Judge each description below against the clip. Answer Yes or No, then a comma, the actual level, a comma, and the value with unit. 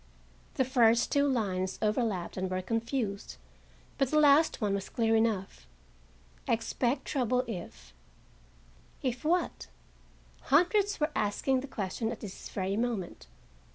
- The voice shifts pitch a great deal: Yes, wide, 5.7 semitones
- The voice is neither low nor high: No, high, 225 Hz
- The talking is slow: Yes, slow, 125 wpm